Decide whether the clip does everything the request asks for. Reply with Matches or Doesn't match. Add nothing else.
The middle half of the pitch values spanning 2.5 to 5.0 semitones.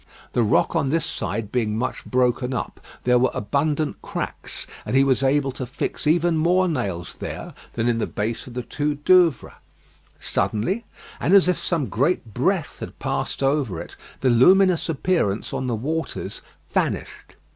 Doesn't match